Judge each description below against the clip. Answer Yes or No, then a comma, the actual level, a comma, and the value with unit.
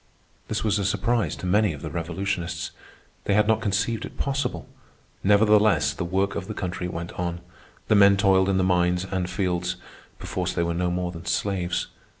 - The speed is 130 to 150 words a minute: No, average, 180 wpm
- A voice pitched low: Yes, very low, 95 Hz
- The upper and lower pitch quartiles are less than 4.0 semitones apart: Yes, average, 2.7 semitones